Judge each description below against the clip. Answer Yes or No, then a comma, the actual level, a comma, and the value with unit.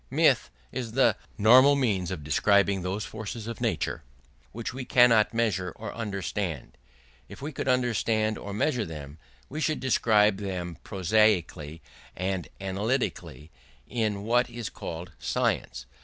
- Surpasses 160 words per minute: No, slow, 135 wpm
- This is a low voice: Yes, low, 105 Hz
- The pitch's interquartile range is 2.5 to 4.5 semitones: Yes, average, 4.0 semitones